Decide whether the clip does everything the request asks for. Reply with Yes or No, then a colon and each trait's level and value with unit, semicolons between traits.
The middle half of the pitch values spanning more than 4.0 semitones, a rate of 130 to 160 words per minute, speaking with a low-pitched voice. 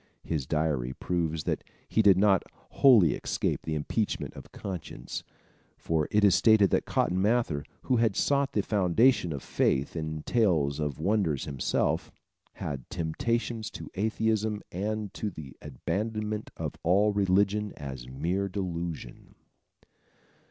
Yes: wide, 5.5 semitones; average, 140 wpm; very low, 95 Hz